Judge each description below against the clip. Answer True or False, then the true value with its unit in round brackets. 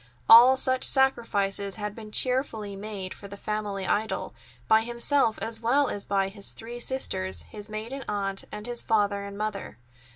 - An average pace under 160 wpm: False (165 wpm)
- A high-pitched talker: True (215 Hz)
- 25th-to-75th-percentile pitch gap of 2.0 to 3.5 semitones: True (2.9 semitones)